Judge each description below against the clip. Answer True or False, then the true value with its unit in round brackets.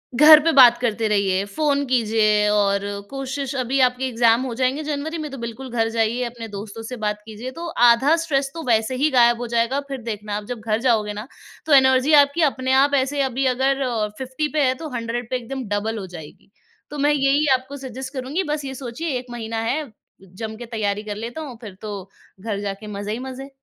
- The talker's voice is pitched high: True (250 Hz)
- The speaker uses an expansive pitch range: False (3.7 semitones)